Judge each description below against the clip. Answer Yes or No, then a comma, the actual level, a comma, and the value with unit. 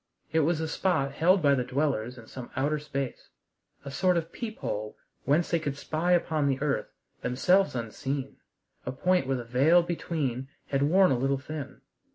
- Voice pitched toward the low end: No, medium, 145 Hz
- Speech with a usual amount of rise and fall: Yes, average, 4.0 semitones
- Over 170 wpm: Yes, average, 180 wpm